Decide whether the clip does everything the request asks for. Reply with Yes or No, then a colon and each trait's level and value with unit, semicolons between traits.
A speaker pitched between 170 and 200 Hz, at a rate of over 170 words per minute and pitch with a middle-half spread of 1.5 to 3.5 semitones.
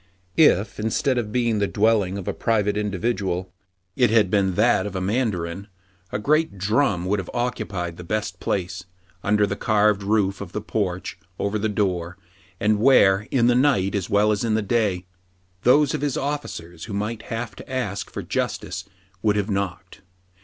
No: low, 105 Hz; average, 180 wpm; average, 3.0 semitones